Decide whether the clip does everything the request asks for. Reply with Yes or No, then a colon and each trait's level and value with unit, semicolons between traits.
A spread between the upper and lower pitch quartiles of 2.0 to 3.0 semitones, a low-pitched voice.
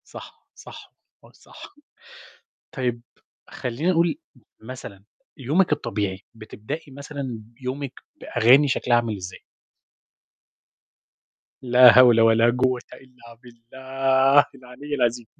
Yes: narrow, 2.6 semitones; low, 125 Hz